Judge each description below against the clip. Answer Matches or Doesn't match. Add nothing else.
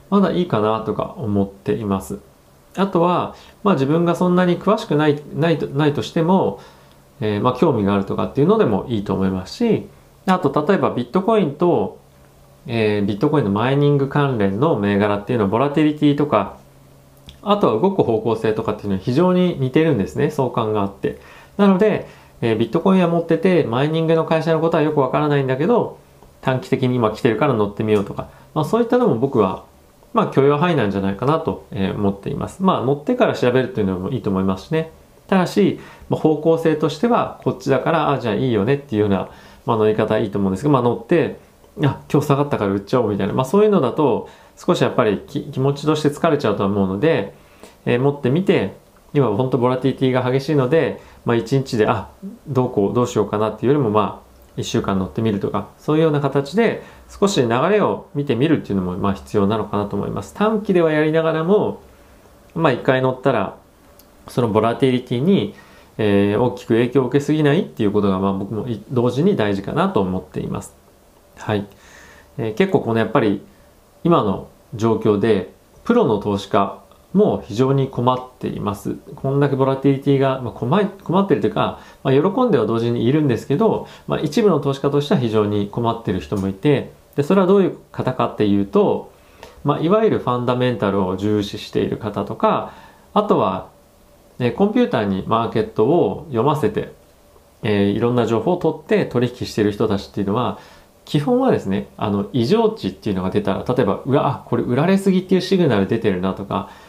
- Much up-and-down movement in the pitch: Matches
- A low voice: Matches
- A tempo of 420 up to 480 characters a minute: Matches